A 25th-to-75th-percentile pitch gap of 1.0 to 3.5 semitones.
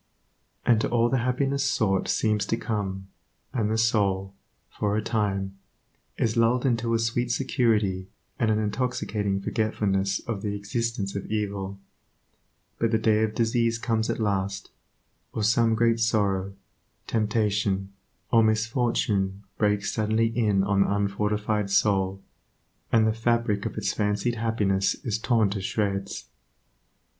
Yes: narrow, 2.5 semitones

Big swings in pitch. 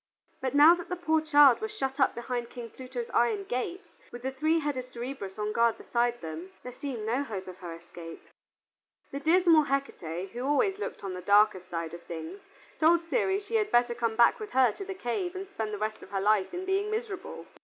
Yes: wide, 7.3 semitones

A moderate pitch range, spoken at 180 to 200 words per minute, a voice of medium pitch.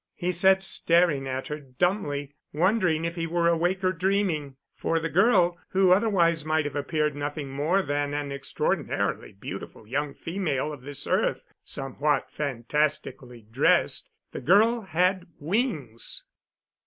No: average, 4.2 semitones; average, 140 wpm; medium, 155 Hz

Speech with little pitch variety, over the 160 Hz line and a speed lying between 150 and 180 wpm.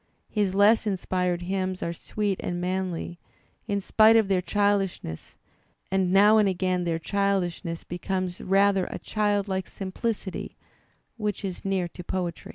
No: narrow, 2.0 semitones; high, 190 Hz; average, 140 wpm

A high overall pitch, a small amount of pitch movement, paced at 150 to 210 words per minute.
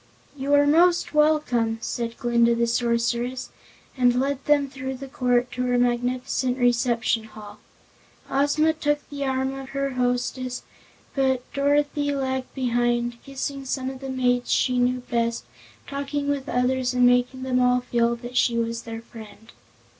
Yes: very high, 250 Hz; narrow, 2.2 semitones; average, 155 wpm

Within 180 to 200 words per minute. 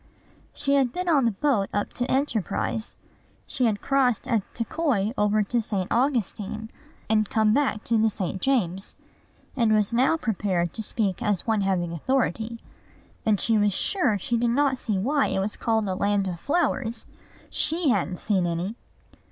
No: average, 170 wpm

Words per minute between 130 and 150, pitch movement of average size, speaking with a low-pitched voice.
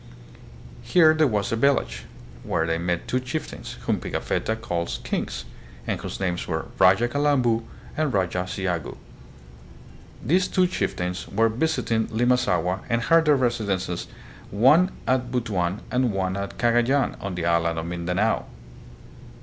No: average, 140 wpm; wide, 6.0 semitones; low, 110 Hz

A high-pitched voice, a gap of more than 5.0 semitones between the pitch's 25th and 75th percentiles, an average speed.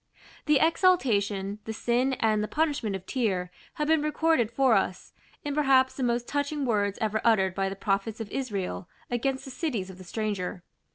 Yes: high, 230 Hz; wide, 5.4 semitones; average, 180 wpm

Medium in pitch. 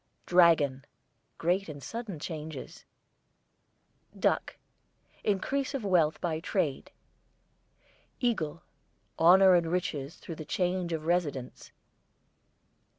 Yes: medium, 170 Hz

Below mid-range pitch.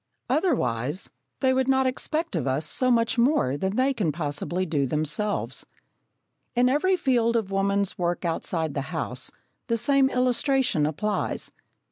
No: high, 210 Hz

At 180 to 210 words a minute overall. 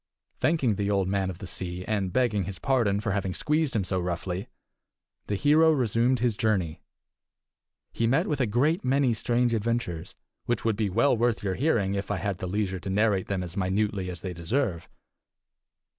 Yes: average, 185 wpm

